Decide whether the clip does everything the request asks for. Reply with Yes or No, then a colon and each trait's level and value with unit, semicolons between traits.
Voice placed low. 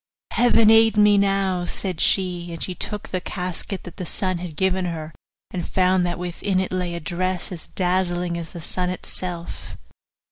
No: medium, 180 Hz